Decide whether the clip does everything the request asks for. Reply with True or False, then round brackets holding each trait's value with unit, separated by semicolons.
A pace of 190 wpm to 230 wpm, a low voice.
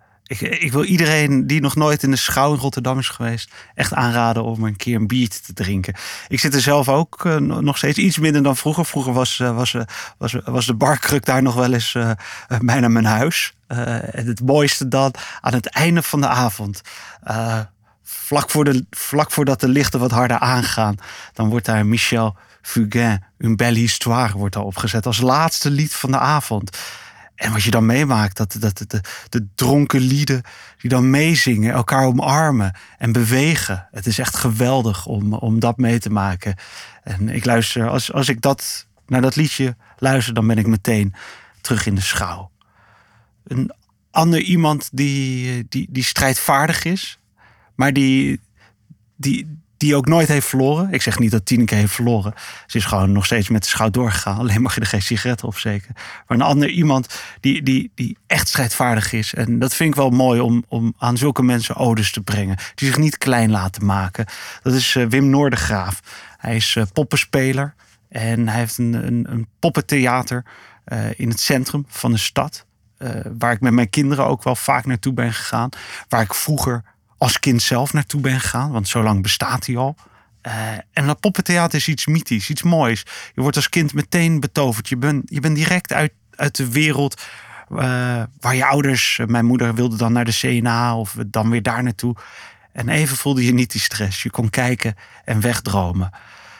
True (195 wpm; 125 Hz)